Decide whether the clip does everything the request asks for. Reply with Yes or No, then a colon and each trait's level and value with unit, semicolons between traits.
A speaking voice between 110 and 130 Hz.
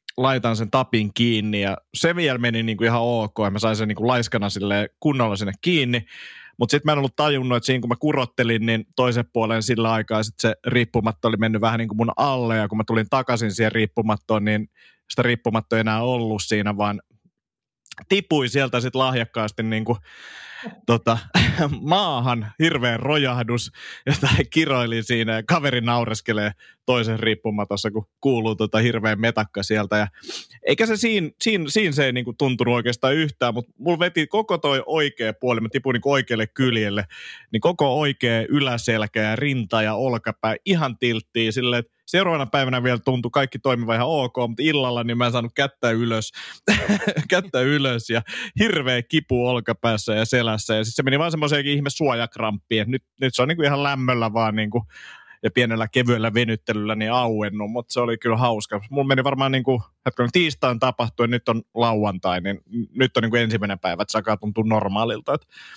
Yes: low, 120 Hz